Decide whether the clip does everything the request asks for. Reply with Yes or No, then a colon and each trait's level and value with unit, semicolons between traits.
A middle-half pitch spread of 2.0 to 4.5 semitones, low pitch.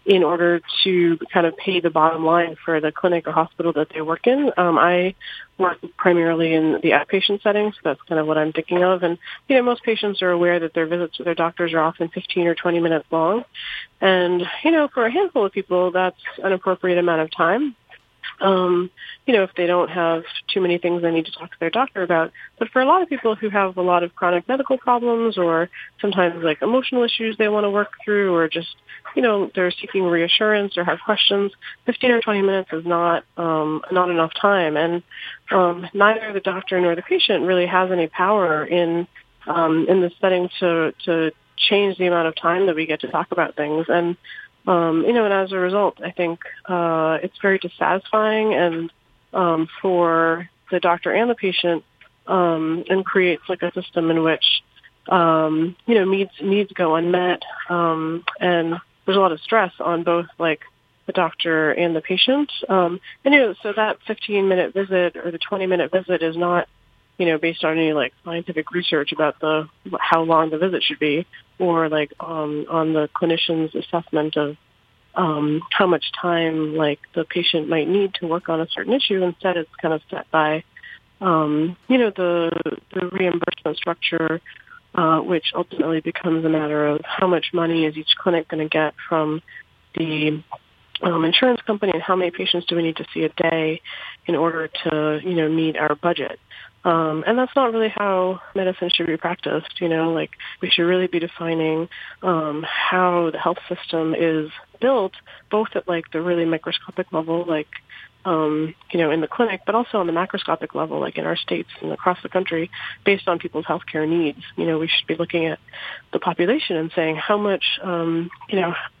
No: average, 2.7 semitones; medium, 175 Hz